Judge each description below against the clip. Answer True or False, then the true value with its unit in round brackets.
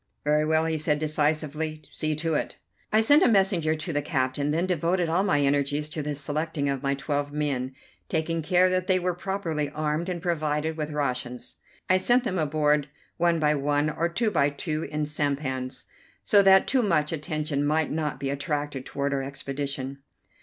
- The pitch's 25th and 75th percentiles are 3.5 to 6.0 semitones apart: False (2.6 semitones)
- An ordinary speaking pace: True (185 wpm)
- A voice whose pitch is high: False (150 Hz)